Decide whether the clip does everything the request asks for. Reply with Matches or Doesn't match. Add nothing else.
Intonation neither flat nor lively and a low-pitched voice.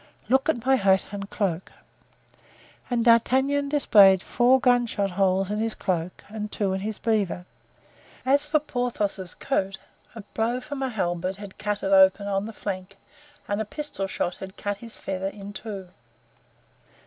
Doesn't match